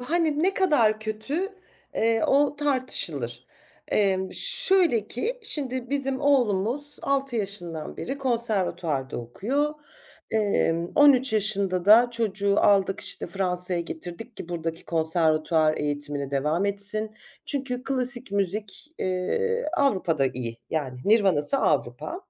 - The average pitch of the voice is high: Yes, high, 210 Hz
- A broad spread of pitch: Yes, wide, 7.8 semitones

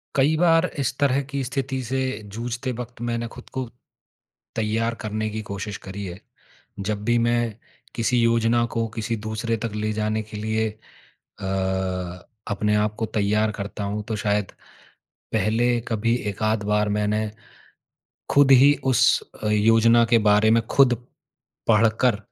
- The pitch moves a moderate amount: No, narrow, 2.2 semitones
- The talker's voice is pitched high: No, low, 115 Hz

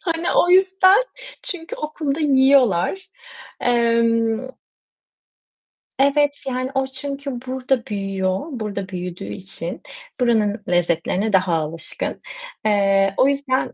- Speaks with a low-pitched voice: No, high, 245 Hz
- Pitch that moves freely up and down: Yes, wide, 6.2 semitones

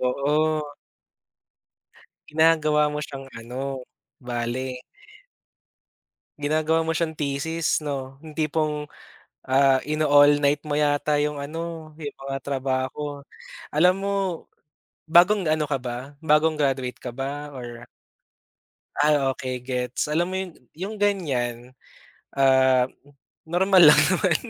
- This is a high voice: No, medium, 145 Hz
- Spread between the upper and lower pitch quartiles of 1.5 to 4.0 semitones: Yes, average, 2.9 semitones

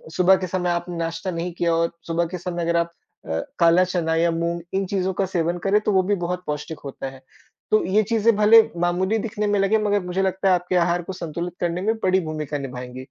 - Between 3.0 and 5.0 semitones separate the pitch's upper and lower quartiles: No, narrow, 2.4 semitones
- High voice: No, medium, 175 Hz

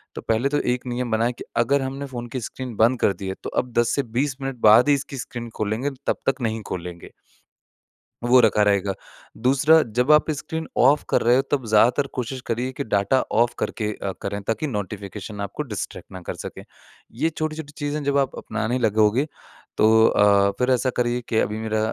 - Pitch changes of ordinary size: Yes, average, 4.0 semitones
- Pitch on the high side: No, low, 120 Hz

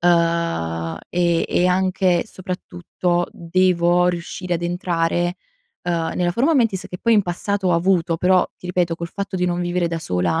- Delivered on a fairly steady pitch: Yes, narrow, 1.4 semitones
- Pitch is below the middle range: No, medium, 175 Hz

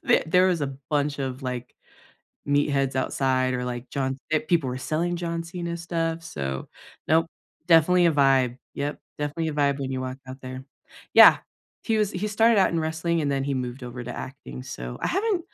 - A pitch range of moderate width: Yes, average, 4.5 semitones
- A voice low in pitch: No, medium, 145 Hz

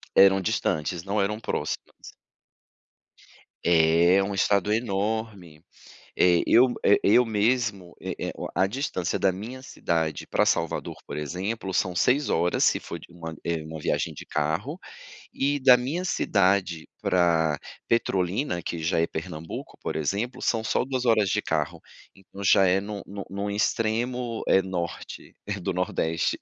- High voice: No, very low, 95 Hz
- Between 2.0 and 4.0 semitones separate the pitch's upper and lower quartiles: No, average, 4.6 semitones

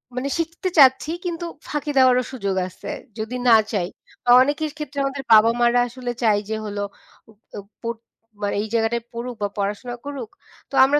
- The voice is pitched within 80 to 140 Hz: No, high, 245 Hz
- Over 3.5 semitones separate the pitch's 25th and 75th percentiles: Yes, average, 4.2 semitones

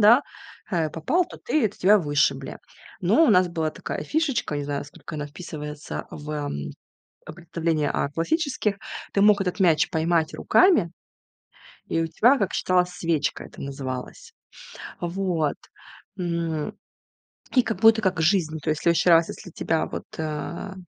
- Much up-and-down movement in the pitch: No, average, 4.5 semitones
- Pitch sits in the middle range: Yes, medium, 170 Hz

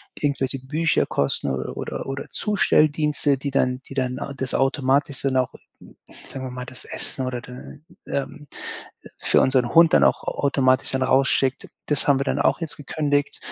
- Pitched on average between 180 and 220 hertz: No, low, 135 Hz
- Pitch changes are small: Yes, narrow, 1.9 semitones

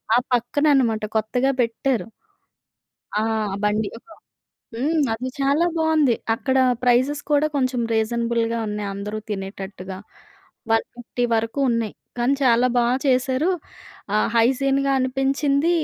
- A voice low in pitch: No, high, 245 Hz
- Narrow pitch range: No, average, 3.4 semitones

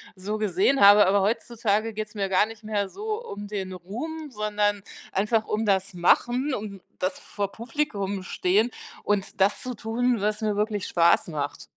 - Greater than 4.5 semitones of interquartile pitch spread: No, narrow, 2.5 semitones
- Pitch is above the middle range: Yes, high, 210 Hz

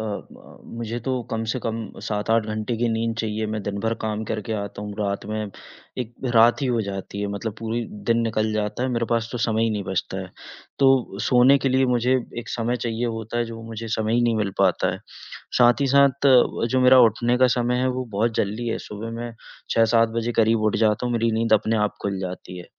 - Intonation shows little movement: Yes, narrow, 2.0 semitones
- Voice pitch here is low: Yes, low, 115 Hz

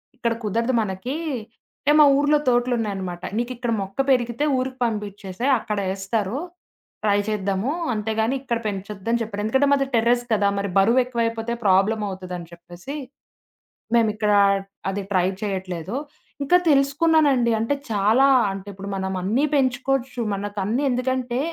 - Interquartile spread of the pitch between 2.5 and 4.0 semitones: No, average, 4.5 semitones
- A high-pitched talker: Yes, high, 225 Hz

